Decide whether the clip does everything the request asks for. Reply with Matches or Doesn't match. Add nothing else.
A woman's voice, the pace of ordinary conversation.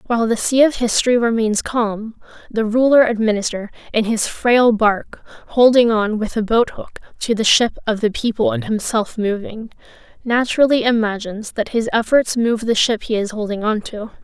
Matches